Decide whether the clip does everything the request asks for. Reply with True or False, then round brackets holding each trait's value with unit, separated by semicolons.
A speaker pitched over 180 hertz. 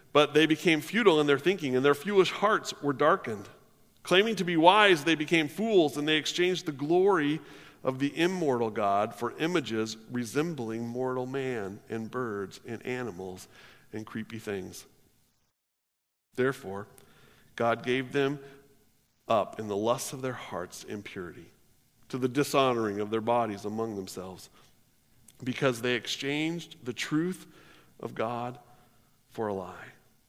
False (130 Hz)